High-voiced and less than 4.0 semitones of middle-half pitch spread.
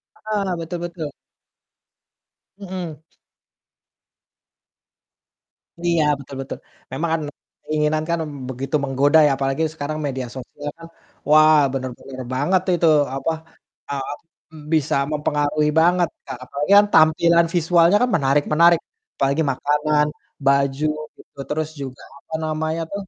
No: medium, 155 Hz; average, 3.1 semitones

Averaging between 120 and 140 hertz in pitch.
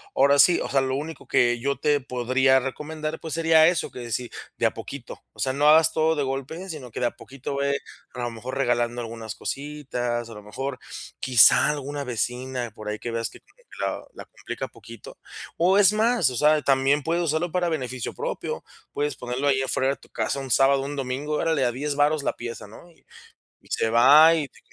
Yes: low, 135 Hz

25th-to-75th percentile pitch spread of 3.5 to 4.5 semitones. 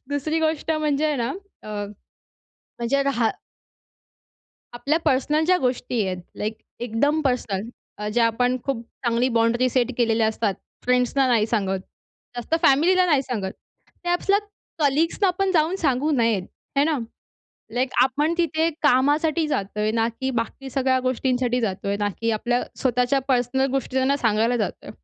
Yes: average, 4.2 semitones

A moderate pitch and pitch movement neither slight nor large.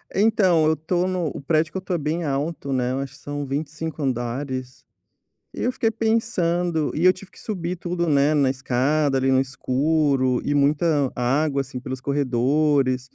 Yes: medium, 145 Hz; average, 4.1 semitones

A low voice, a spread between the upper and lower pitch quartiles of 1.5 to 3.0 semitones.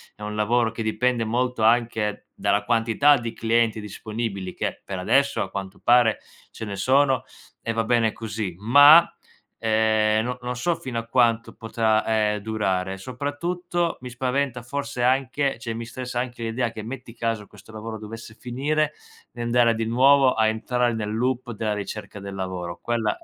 Yes: low, 115 Hz; narrow, 2.6 semitones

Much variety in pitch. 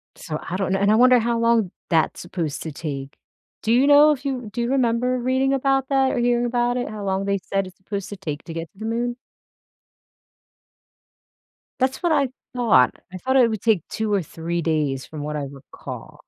Yes: wide, 6.5 semitones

